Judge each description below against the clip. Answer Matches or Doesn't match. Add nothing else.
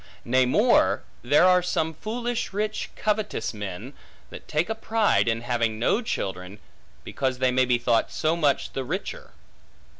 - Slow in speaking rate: Doesn't match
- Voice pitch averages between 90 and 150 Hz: Matches